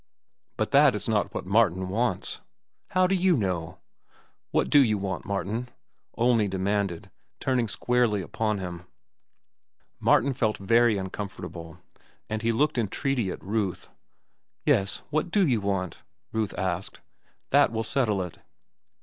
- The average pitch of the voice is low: Yes, low, 105 Hz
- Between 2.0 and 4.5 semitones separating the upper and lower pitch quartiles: Yes, average, 4.2 semitones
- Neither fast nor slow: No, slow, 130 wpm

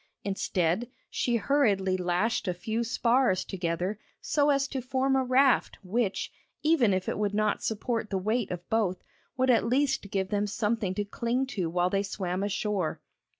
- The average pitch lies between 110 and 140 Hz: No, high, 210 Hz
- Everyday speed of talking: Yes, average, 170 wpm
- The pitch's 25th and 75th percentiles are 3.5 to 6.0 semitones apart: Yes, average, 4.7 semitones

